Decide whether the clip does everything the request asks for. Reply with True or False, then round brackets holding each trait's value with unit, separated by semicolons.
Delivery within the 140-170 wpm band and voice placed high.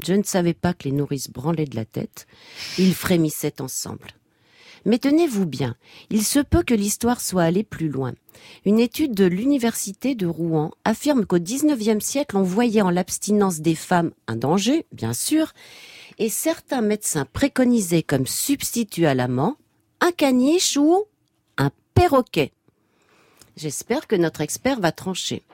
True (155 wpm; 195 Hz)